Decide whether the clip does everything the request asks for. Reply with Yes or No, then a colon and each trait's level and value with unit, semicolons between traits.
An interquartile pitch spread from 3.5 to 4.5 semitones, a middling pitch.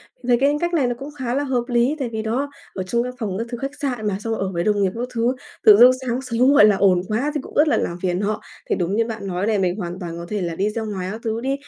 No: average, 4.2 semitones; high, 225 Hz